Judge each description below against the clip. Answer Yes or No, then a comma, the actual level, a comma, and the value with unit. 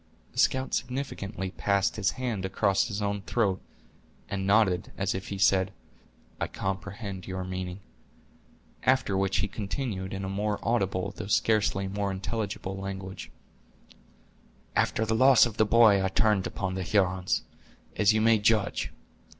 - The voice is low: Yes, low, 100 Hz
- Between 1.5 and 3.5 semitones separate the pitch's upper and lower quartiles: Yes, narrow, 2.4 semitones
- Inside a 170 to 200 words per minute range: No, average, 150 wpm